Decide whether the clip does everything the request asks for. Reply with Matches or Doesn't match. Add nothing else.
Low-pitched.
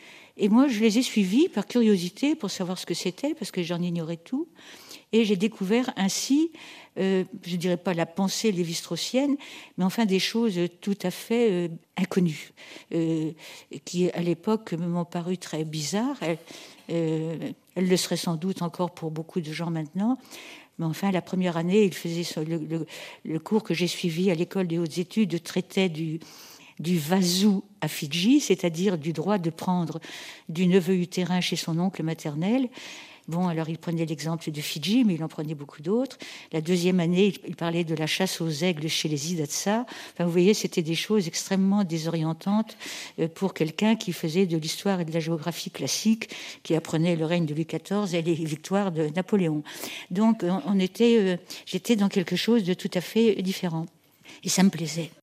Doesn't match